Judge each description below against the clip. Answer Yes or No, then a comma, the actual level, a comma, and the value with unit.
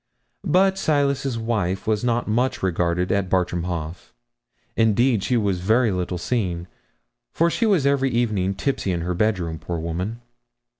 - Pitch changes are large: Yes, wide, 5.8 semitones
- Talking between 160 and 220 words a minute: No, average, 150 wpm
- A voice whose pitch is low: Yes, low, 105 Hz